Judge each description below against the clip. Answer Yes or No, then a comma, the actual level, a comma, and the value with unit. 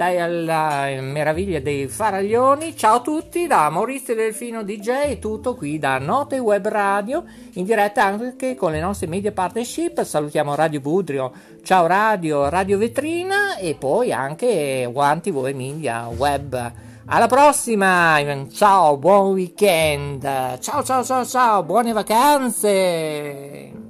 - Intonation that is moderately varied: No, wide, 8.2 semitones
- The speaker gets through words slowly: Yes, slow, 130 wpm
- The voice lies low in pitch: No, high, 195 Hz